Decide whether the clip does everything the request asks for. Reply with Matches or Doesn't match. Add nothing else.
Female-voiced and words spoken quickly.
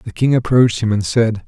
Doesn't match